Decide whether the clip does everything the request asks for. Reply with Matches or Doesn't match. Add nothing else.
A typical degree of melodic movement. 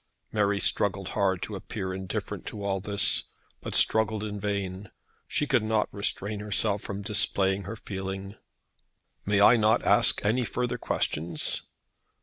Doesn't match